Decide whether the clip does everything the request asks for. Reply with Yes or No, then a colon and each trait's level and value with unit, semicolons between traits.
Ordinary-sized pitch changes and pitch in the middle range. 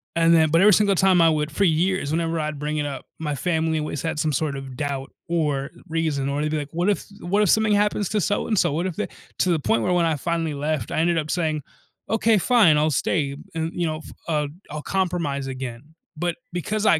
Yes: average, 3.0 semitones; medium, 160 Hz